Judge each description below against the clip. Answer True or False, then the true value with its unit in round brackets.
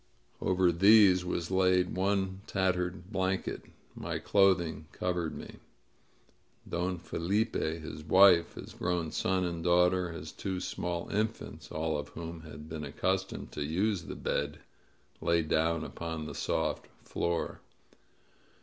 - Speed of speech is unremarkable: False (130 wpm)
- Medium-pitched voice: False (90 Hz)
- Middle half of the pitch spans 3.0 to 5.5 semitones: False (2.4 semitones)